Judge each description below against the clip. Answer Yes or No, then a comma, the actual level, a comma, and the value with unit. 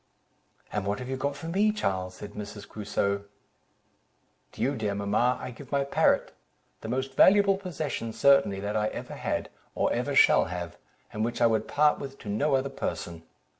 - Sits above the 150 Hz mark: No, low, 120 Hz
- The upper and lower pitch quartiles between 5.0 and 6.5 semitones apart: Yes, wide, 5.4 semitones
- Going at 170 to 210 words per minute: Yes, average, 185 wpm